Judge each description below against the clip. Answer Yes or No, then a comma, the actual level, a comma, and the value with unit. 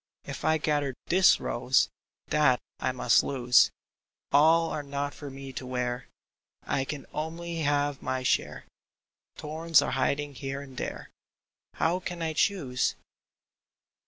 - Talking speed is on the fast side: No, slow, 135 wpm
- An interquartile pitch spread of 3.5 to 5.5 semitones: No, average, 3.1 semitones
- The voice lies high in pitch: No, medium, 145 Hz